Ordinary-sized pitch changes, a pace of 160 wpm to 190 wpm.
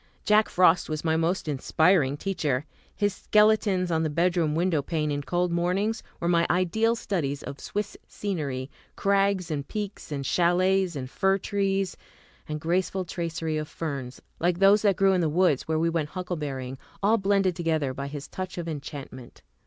Yes: average, 4.2 semitones; average, 170 wpm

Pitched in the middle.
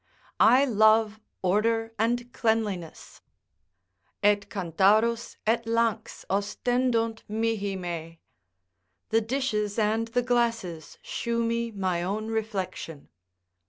No: high, 220 Hz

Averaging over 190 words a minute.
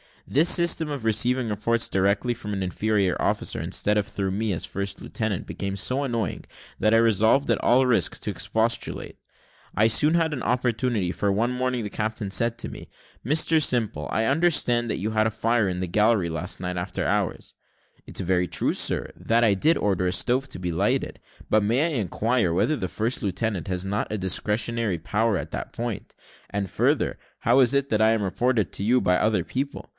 Yes: average, 200 wpm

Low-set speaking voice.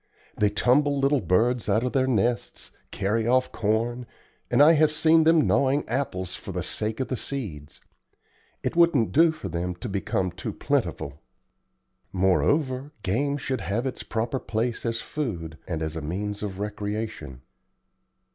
Yes: low, 115 Hz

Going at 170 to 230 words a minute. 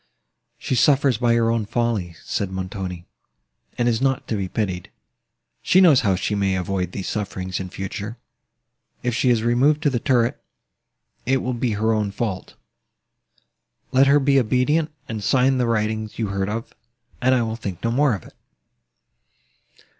No: average, 160 wpm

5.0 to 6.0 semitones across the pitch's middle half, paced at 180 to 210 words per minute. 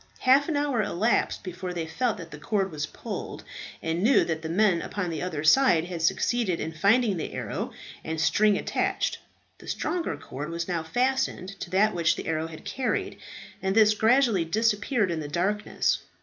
Yes: average, 5.3 semitones; average, 185 wpm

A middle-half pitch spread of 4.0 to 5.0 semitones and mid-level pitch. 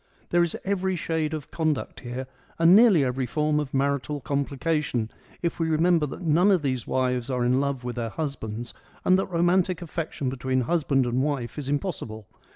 Yes: average, 4.5 semitones; medium, 145 Hz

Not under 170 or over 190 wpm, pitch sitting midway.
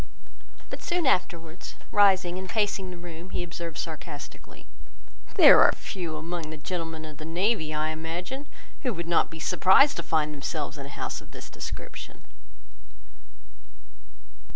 No: average, 150 wpm; medium, 170 Hz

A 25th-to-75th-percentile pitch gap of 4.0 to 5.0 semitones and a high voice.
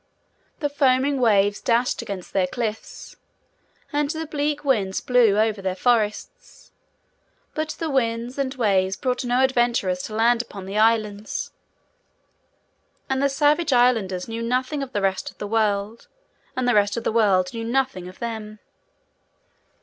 Yes: average, 4.3 semitones; high, 230 Hz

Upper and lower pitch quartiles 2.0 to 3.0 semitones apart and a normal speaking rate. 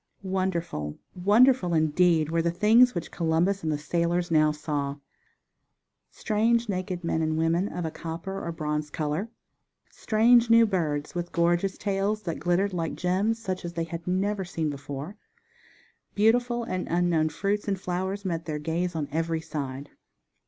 No: average, 3.6 semitones; average, 155 wpm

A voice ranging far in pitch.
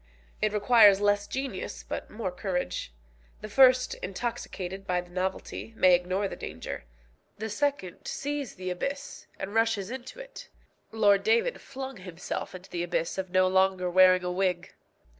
No: average, 4.7 semitones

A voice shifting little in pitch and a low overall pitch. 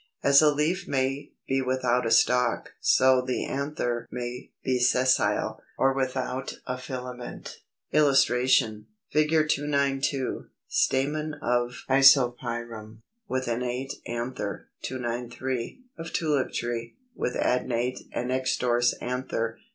Yes: narrow, 2.0 semitones; low, 130 Hz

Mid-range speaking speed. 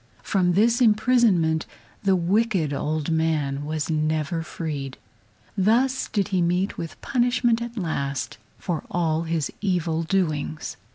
No: slow, 125 wpm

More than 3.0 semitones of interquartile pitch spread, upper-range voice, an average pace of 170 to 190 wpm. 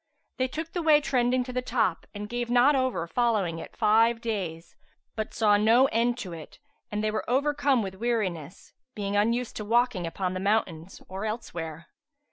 Yes: average, 4.4 semitones; high, 220 Hz; average, 175 wpm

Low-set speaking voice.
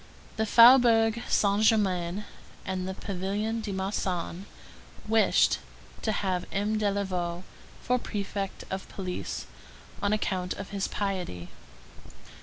No: high, 200 Hz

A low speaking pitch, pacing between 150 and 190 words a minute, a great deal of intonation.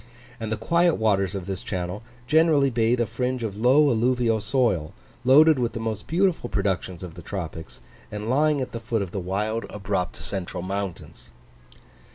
No: low, 110 Hz; average, 175 wpm; average, 4.7 semitones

